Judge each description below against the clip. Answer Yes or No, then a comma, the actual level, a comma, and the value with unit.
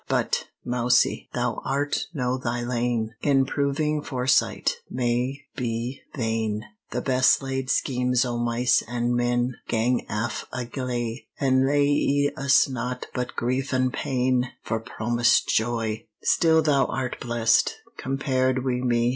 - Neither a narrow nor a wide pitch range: No, narrow, 1.9 semitones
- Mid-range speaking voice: No, low, 125 Hz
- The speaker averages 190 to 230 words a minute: No, slow, 135 wpm